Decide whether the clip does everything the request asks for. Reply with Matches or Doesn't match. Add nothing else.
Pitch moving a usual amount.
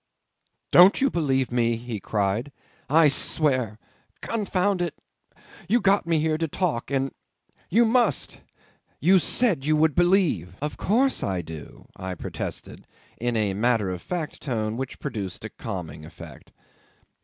Doesn't match